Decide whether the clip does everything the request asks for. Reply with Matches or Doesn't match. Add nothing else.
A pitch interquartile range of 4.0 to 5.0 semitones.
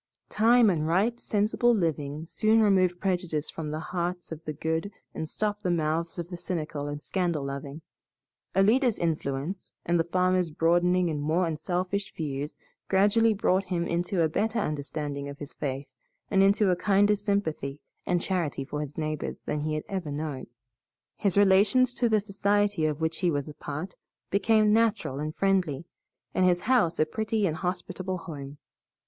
Matches